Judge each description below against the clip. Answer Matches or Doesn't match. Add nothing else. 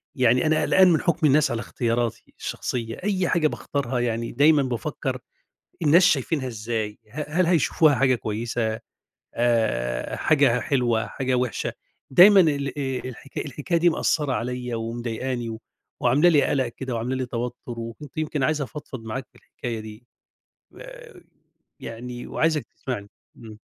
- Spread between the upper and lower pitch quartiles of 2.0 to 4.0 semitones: Doesn't match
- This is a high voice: Doesn't match